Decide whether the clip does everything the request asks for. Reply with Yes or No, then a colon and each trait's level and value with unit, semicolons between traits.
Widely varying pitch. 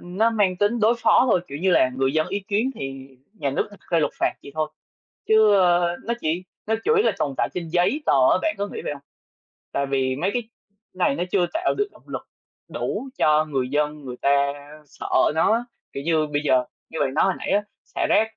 Yes: wide, 6.6 semitones